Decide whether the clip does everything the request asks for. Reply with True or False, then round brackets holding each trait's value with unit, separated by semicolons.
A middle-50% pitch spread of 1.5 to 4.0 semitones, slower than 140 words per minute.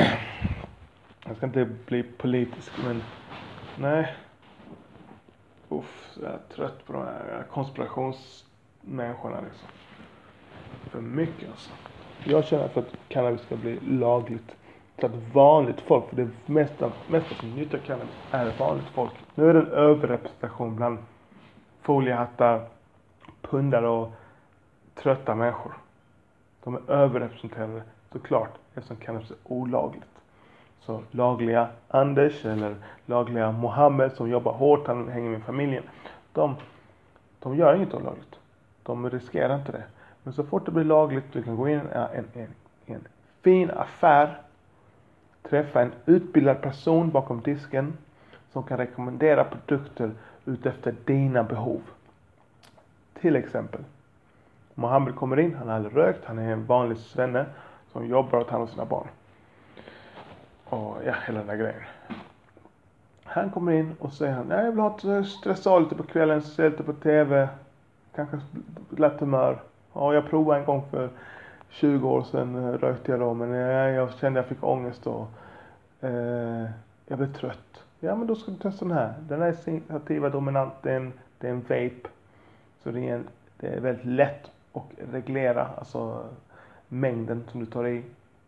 False (3.6 semitones; 145 wpm)